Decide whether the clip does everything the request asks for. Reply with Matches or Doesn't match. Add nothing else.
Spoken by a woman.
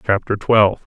Doesn't match